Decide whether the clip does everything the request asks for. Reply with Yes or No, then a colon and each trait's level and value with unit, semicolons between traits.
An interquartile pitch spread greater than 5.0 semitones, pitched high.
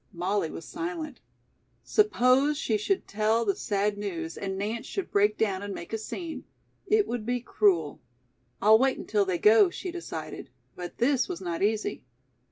Yes: wide, 5.4 semitones; high, 215 Hz